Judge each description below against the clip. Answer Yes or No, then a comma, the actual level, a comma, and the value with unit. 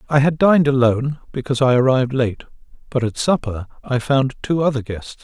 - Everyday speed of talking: Yes, average, 185 wpm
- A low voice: Yes, low, 130 Hz